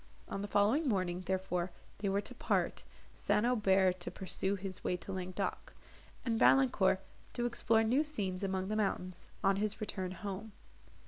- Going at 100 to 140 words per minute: No, average, 165 wpm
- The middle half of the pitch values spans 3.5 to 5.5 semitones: No, narrow, 2.6 semitones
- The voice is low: No, high, 195 Hz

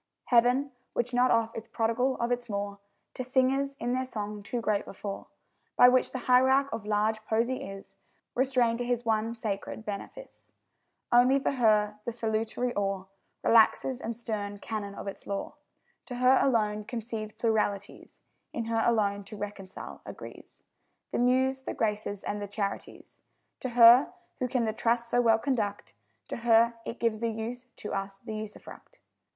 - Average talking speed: Yes, average, 165 wpm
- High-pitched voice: Yes, high, 230 Hz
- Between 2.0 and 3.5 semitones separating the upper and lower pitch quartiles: Yes, average, 2.8 semitones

